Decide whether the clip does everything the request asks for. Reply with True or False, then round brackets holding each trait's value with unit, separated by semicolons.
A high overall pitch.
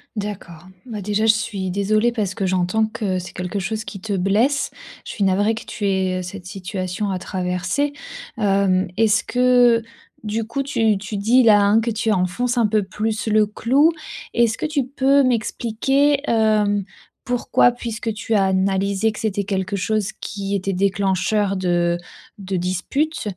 True (210 Hz)